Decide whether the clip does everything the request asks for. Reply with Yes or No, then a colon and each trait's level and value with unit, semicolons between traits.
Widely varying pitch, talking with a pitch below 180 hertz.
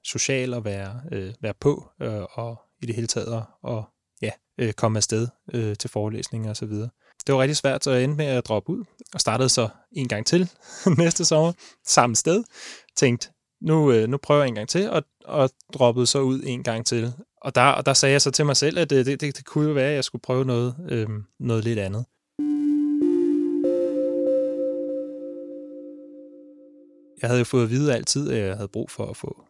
Yes: wide, 6.9 semitones; low, 135 Hz